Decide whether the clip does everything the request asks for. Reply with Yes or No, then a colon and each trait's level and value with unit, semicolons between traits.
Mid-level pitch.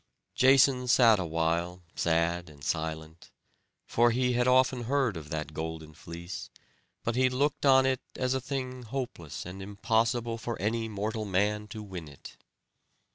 No: low, 110 Hz